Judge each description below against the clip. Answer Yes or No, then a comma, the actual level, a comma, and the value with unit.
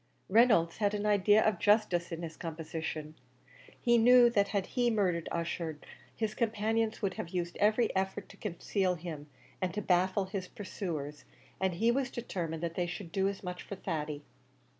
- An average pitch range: Yes, average, 4.0 semitones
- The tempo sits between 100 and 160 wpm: No, average, 175 wpm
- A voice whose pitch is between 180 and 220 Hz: Yes, high, 190 Hz